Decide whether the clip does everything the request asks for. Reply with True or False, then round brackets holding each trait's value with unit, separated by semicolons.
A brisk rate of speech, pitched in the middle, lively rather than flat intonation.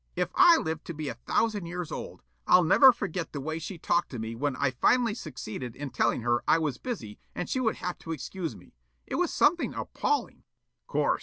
True (215 wpm; 165 Hz; 7.5 semitones)